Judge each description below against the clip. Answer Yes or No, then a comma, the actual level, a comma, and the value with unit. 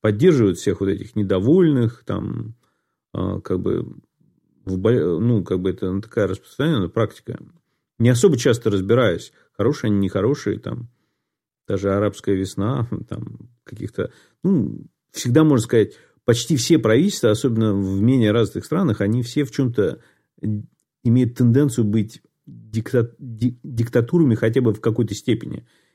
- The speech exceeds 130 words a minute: No, average, 125 wpm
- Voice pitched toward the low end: Yes, low, 115 Hz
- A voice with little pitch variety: No, average, 3.7 semitones